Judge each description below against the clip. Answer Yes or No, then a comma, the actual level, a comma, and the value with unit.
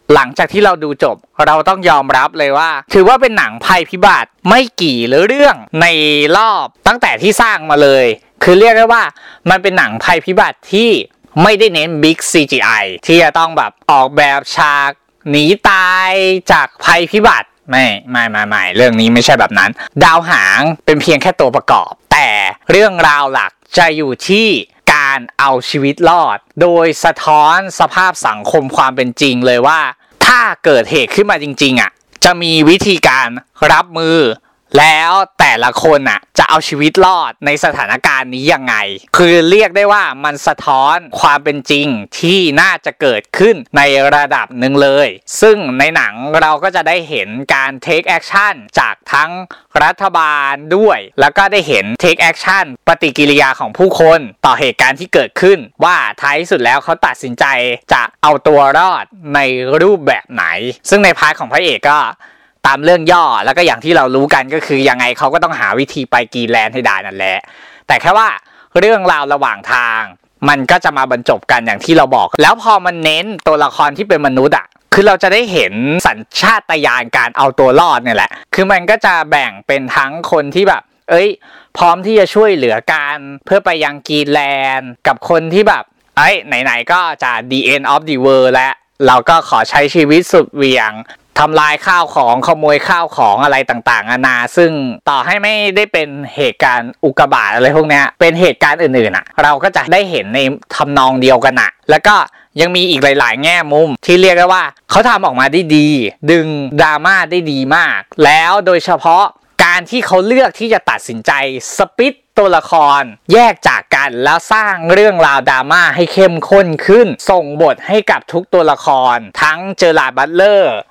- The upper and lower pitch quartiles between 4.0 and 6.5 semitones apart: Yes, average, 5.1 semitones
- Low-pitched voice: No, medium, 155 Hz